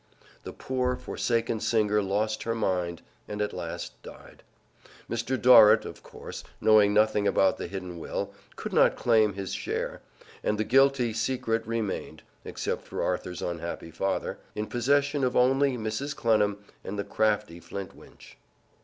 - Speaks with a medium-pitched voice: No, low, 110 Hz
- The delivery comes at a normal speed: Yes, average, 145 wpm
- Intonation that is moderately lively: Yes, average, 3.4 semitones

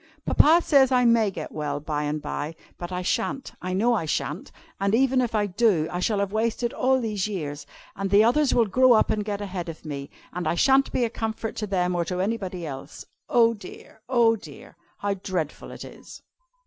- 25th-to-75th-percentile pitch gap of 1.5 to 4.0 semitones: No, average, 4.8 semitones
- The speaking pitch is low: No, high, 205 Hz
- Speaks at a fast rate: Yes, fast, 210 wpm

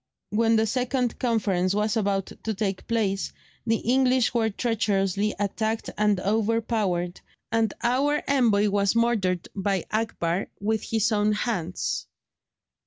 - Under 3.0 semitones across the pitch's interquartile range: Yes, narrow, 2.6 semitones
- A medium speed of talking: No, slow, 125 wpm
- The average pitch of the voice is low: No, high, 215 Hz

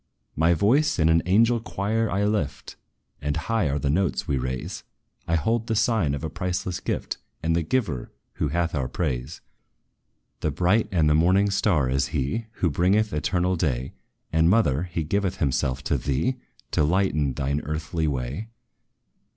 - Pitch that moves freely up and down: Yes, wide, 5.7 semitones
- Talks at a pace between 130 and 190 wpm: Yes, average, 165 wpm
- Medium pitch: No, very low, 85 Hz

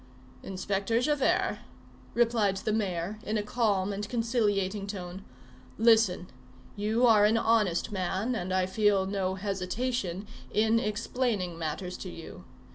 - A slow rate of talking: Yes, slow, 125 wpm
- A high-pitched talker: Yes, high, 205 Hz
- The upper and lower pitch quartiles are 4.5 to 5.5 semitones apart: No, average, 3.2 semitones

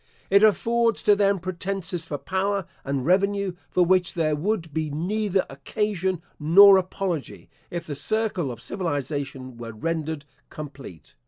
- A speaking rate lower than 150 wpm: Yes, average, 140 wpm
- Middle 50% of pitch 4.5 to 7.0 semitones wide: Yes, average, 5.1 semitones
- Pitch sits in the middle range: Yes, medium, 175 Hz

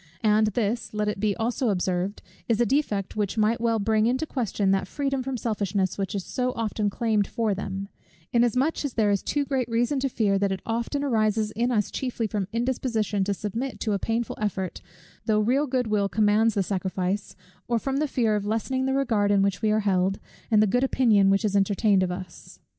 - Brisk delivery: Yes, fast, 210 wpm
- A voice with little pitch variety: No, average, 3.2 semitones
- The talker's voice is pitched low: No, high, 215 Hz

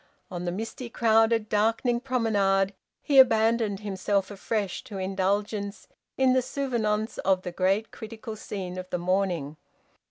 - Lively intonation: No, average, 2.9 semitones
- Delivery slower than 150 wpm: Yes, slow, 135 wpm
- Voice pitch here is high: Yes, high, 210 Hz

